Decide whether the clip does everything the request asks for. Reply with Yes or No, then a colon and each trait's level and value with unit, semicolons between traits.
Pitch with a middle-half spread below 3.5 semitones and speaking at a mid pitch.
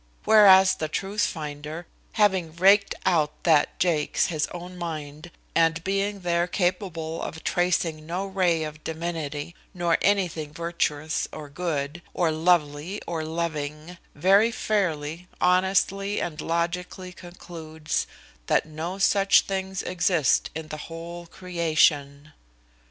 Yes: average, 2.9 semitones; medium, 170 Hz